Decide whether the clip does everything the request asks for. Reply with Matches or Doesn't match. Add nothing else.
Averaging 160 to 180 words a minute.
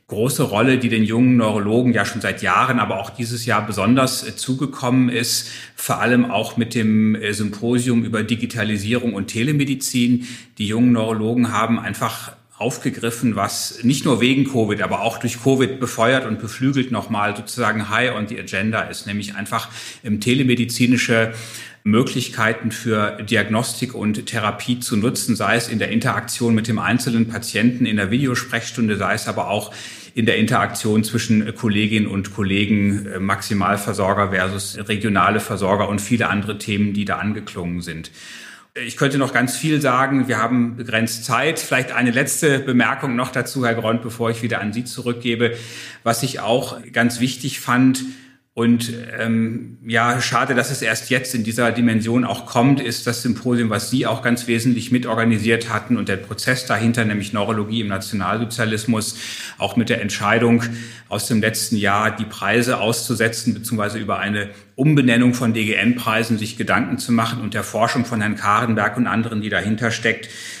Matches